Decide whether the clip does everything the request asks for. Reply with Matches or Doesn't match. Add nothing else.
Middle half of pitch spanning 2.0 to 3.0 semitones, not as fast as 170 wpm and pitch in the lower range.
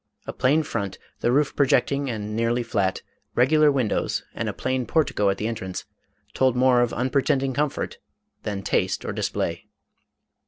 Doesn't match